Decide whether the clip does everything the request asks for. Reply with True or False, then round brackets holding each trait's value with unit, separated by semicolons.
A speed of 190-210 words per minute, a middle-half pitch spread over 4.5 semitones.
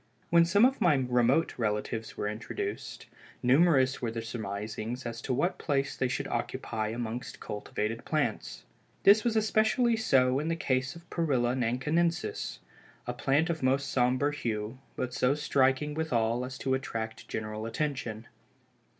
False (150 wpm; 5.1 semitones)